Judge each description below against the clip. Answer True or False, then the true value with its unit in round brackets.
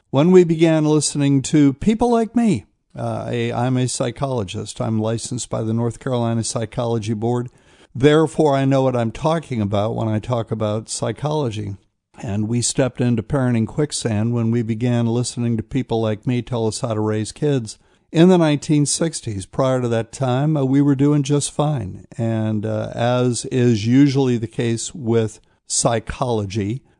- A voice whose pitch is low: True (120 Hz)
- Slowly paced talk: False (165 wpm)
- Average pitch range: True (3.9 semitones)